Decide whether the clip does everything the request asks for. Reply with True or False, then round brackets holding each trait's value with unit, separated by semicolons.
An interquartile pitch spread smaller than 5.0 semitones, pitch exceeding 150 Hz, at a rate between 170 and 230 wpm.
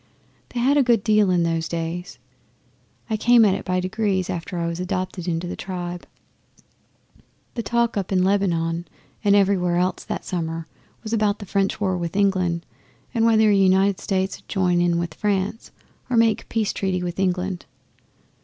True (2.8 semitones; 190 Hz; 180 wpm)